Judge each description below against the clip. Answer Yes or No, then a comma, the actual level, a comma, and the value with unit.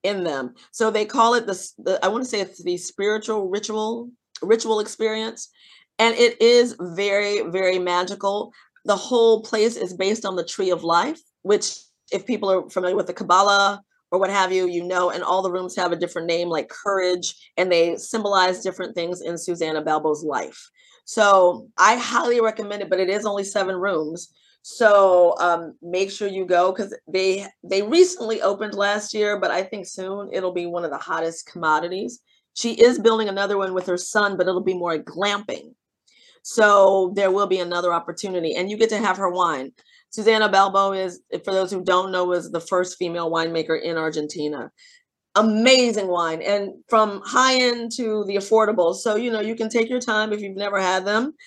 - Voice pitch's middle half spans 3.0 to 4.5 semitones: Yes, average, 3.5 semitones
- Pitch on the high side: Yes, high, 195 Hz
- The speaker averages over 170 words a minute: Yes, average, 190 wpm